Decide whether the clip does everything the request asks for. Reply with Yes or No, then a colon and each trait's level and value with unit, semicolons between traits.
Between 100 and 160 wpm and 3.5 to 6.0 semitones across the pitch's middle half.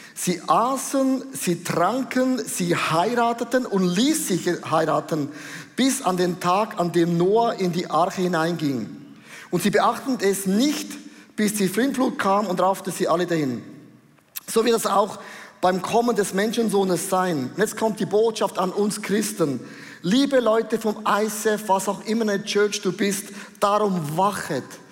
Yes: average, 155 wpm; average, 3.9 semitones